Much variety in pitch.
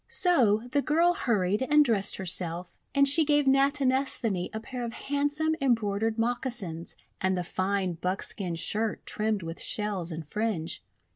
Yes: wide, 6.6 semitones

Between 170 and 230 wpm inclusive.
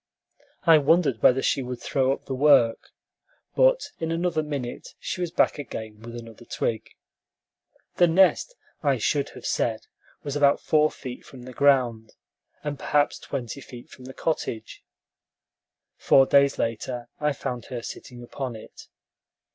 No: average, 150 wpm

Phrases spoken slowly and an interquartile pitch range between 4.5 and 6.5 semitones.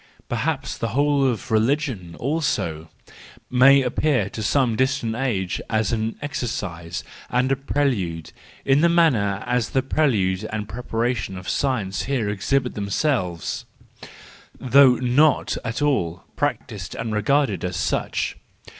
Yes: slow, 130 wpm; average, 5.3 semitones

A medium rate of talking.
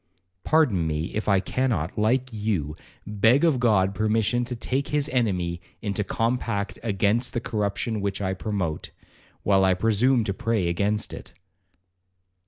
Yes: average, 145 wpm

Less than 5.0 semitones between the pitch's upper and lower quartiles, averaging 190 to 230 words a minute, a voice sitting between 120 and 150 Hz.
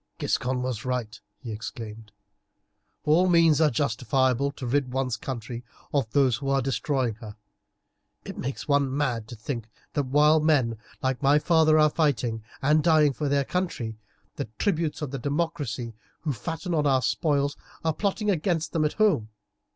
No: average, 3.9 semitones; average, 165 wpm; medium, 140 Hz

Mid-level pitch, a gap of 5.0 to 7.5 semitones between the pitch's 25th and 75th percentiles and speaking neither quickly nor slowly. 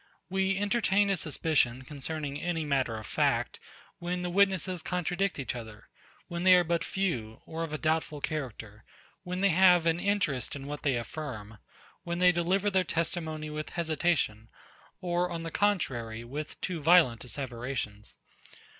Yes: medium, 160 Hz; average, 5.3 semitones; average, 155 wpm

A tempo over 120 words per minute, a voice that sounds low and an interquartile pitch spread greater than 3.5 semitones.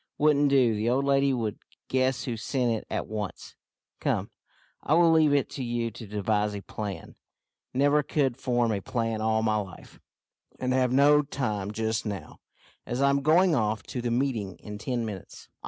Yes: average, 180 wpm; low, 120 Hz; average, 4.4 semitones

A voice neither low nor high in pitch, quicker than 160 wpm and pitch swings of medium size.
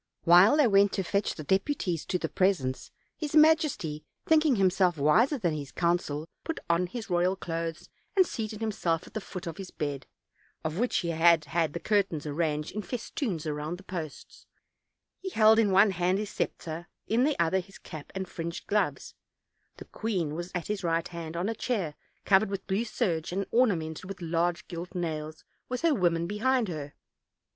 Yes: medium, 180 Hz; average, 185 wpm; average, 4.4 semitones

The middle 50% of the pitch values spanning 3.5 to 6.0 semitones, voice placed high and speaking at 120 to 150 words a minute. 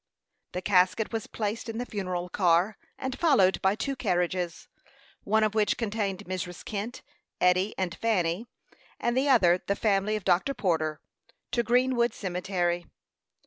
Yes: average, 4.0 semitones; high, 200 Hz; average, 145 wpm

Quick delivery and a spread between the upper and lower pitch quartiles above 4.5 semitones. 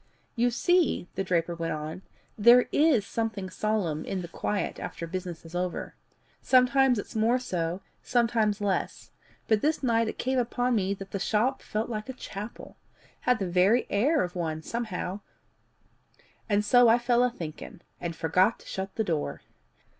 No: average, 170 wpm; average, 5.1 semitones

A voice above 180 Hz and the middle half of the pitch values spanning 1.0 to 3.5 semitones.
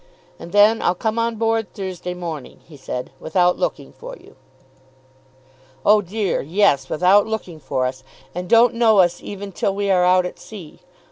No: high, 190 Hz; average, 3.9 semitones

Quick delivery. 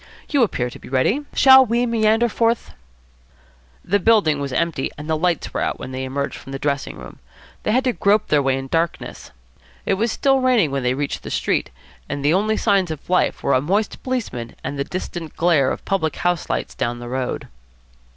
Yes: fast, 210 wpm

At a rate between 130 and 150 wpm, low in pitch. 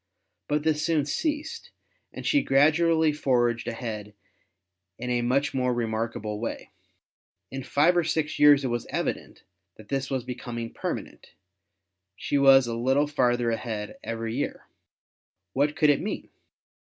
Yes: average, 140 wpm; low, 130 Hz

